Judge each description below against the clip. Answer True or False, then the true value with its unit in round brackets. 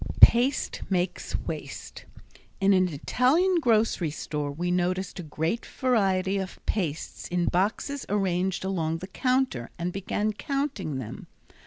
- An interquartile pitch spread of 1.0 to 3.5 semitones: False (4.8 semitones)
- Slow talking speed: True (130 wpm)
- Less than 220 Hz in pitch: True (190 Hz)